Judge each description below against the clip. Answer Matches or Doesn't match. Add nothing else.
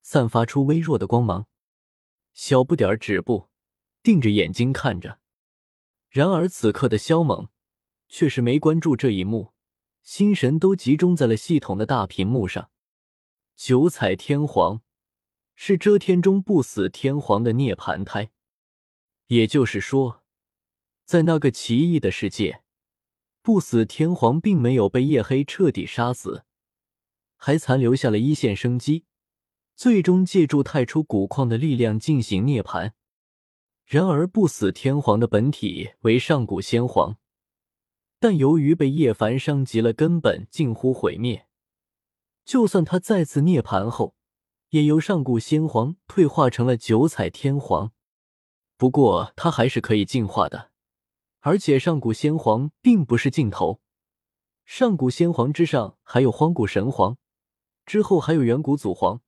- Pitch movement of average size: Doesn't match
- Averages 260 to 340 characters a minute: Doesn't match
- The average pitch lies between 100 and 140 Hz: Matches